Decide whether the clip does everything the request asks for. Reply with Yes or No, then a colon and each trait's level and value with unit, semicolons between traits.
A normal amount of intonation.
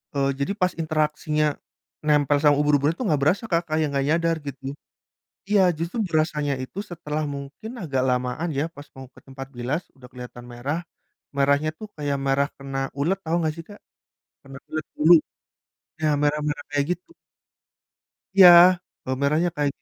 No: narrow, 2.3 semitones